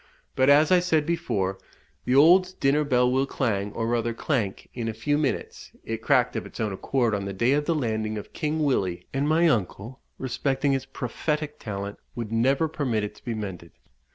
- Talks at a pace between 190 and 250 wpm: Yes, average, 200 wpm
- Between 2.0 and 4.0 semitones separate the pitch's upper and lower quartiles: No, average, 5.3 semitones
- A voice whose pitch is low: Yes, low, 130 Hz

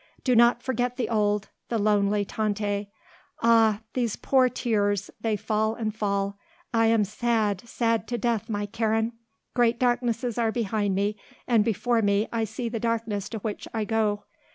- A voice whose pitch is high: Yes, high, 220 Hz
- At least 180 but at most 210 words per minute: No, average, 165 wpm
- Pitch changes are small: Yes, narrow, 2.2 semitones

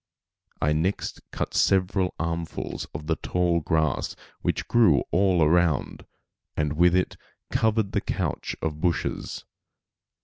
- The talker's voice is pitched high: No, very low, 85 Hz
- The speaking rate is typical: No, slow, 125 wpm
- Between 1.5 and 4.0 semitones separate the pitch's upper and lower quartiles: Yes, average, 2.7 semitones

